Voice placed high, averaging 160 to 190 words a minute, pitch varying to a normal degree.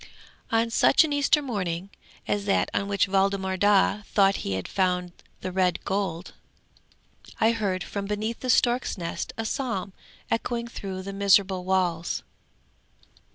No: high, 195 Hz; average, 145 wpm; average, 3.1 semitones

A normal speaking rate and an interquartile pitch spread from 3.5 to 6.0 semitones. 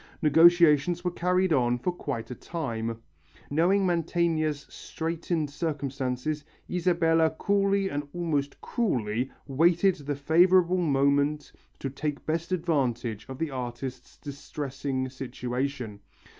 No: slow, 110 wpm; average, 4.3 semitones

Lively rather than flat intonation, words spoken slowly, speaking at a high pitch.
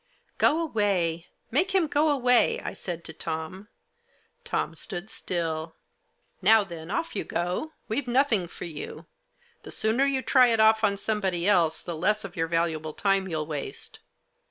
No: wide, 6.4 semitones; average, 175 wpm; high, 195 Hz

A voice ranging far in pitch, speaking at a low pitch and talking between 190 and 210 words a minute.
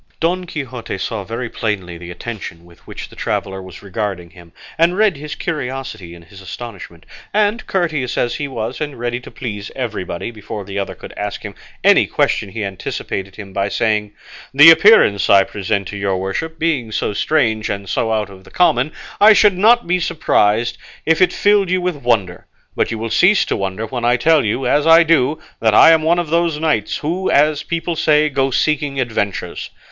Yes: wide, 8.0 semitones; low, 120 Hz; average, 195 wpm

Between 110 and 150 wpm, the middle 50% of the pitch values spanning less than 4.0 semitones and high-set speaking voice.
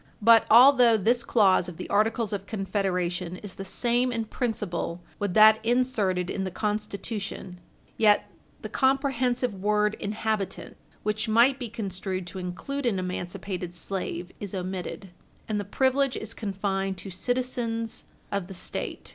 Yes: average, 145 wpm; average, 3.6 semitones; high, 210 Hz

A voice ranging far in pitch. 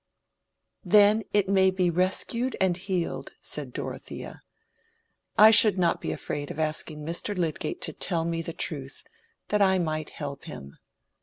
No: average, 3.8 semitones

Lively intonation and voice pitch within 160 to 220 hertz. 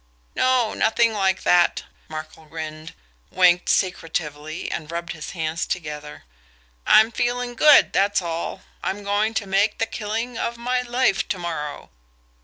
Yes: wide, 5.8 semitones; high, 190 Hz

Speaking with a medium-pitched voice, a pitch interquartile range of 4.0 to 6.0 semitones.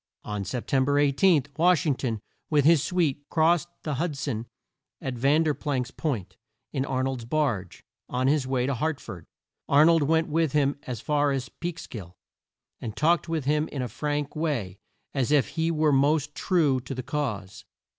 No: medium, 145 Hz; average, 3.4 semitones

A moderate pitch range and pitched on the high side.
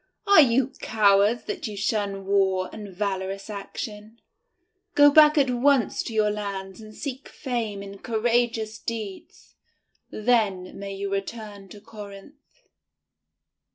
Yes: average, 3.2 semitones; high, 210 Hz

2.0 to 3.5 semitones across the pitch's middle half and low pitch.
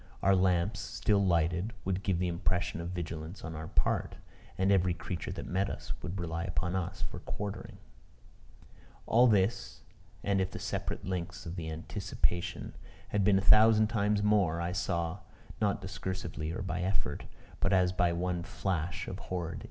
Yes: narrow, 2.5 semitones; very low, 90 Hz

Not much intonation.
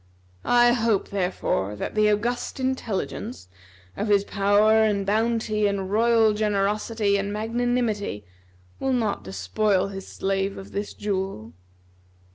Yes: narrow, 2.3 semitones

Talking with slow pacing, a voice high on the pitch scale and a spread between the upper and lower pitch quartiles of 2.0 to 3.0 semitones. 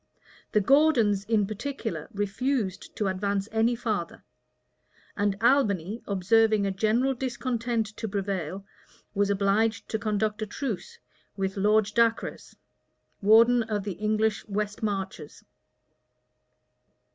Yes: slow, 110 wpm; high, 215 Hz; narrow, 2.4 semitones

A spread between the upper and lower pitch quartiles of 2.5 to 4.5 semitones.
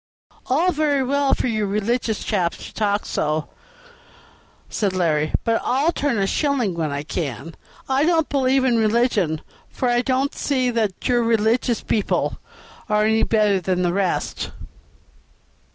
No: average, 5.3 semitones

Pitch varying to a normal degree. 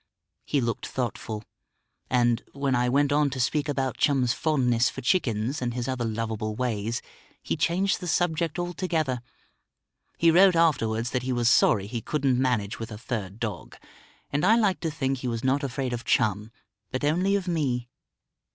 Yes: average, 4.4 semitones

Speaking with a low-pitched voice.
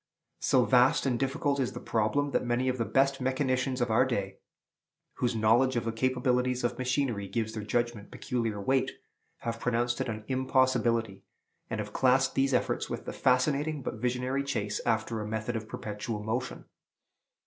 Yes: low, 125 Hz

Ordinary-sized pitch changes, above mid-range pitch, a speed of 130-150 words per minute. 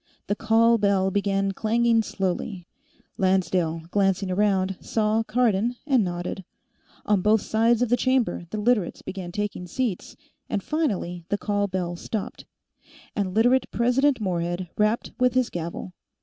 Yes: average, 3.7 semitones; high, 205 Hz; average, 140 wpm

